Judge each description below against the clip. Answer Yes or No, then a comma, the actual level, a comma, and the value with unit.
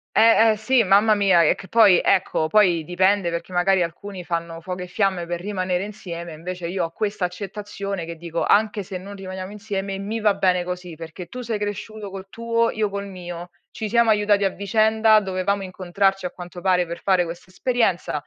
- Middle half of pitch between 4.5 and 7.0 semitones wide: No, average, 2.7 semitones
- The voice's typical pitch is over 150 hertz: Yes, high, 190 Hz